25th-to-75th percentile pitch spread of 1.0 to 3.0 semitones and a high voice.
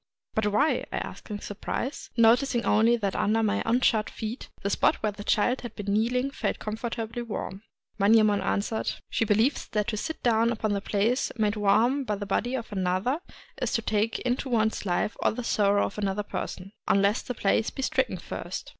Yes: average, 2.7 semitones; high, 220 Hz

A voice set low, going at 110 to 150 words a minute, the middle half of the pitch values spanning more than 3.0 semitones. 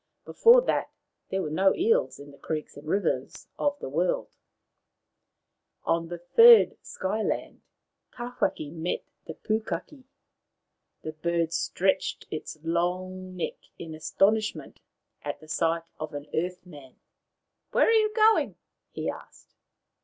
No: medium, 180 Hz; average, 140 wpm; wide, 5.5 semitones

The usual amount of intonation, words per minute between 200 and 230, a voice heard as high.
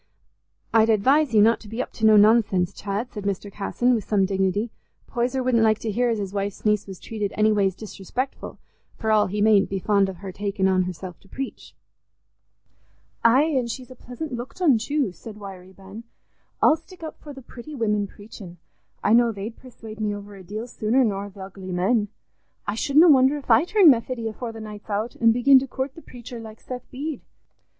Yes: average, 3.7 semitones; fast, 205 wpm; high, 220 Hz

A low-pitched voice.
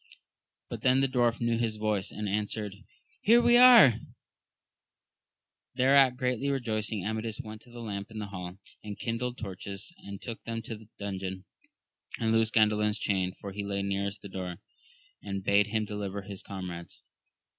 Yes: low, 105 Hz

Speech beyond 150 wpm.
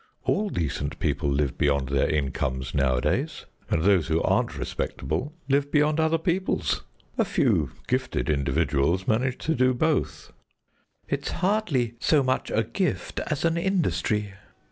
No: average, 140 wpm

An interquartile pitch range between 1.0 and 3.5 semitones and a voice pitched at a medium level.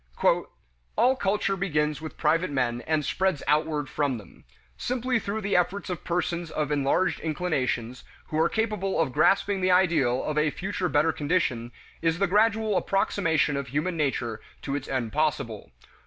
No: average, 4.9 semitones; medium, 160 Hz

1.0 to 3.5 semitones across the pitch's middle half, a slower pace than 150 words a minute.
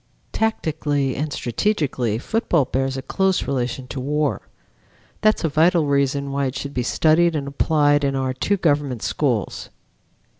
No: average, 2.9 semitones; average, 155 wpm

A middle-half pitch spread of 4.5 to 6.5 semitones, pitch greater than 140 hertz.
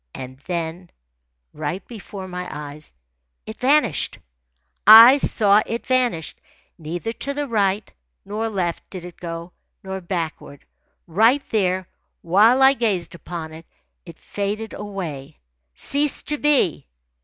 Yes: average, 5.1 semitones; high, 190 Hz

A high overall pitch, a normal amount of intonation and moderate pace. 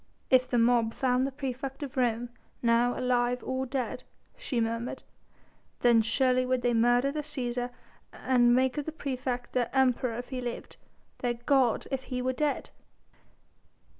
No: very high, 250 Hz; narrow, 1.5 semitones; average, 160 wpm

